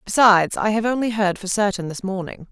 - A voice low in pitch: No, high, 205 Hz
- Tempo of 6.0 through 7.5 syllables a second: No, 5.8 syllables/s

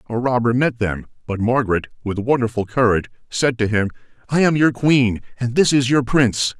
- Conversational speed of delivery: Yes, average, 190 wpm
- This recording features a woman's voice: No, male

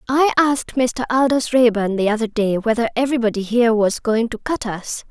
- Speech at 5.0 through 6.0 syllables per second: Yes, 5.5 syllables/s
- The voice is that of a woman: Yes, female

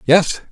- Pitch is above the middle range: No, medium, 165 Hz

